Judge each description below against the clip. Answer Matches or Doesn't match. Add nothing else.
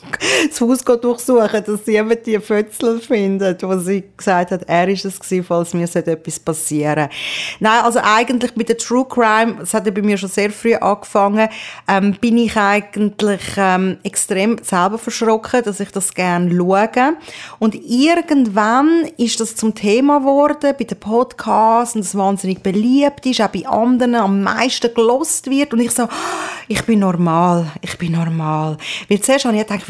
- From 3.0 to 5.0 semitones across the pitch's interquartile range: Matches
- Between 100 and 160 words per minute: Doesn't match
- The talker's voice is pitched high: Matches